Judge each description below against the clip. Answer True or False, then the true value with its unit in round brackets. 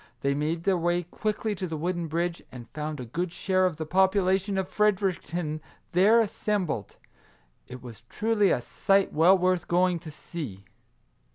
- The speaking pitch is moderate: True (175 Hz)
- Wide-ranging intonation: False (3.7 semitones)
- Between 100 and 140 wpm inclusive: False (170 wpm)